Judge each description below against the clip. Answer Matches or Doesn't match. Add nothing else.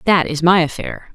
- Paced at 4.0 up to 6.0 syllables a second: Matches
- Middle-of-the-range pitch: Matches